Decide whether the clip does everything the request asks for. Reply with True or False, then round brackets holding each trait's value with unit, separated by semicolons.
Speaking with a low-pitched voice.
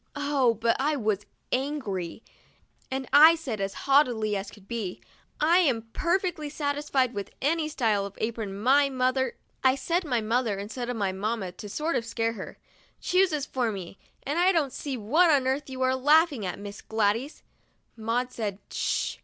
False (255 Hz)